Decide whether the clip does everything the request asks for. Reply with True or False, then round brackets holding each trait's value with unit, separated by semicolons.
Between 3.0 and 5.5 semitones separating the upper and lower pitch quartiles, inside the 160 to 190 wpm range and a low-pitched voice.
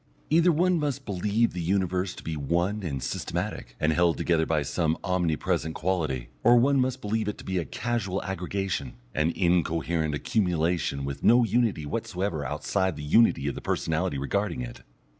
True (5.2 semitones; 170 wpm; 90 Hz)